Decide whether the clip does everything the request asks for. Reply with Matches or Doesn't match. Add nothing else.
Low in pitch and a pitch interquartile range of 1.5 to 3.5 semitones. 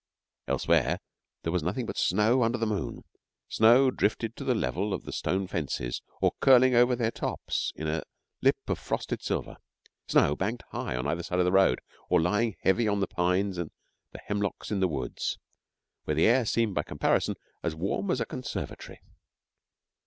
Doesn't match